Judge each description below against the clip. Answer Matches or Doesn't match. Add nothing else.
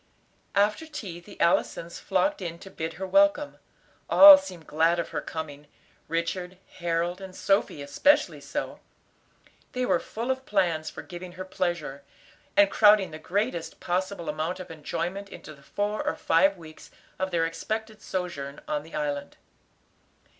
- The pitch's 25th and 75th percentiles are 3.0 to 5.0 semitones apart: Matches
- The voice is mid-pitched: Matches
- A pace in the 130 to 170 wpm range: Matches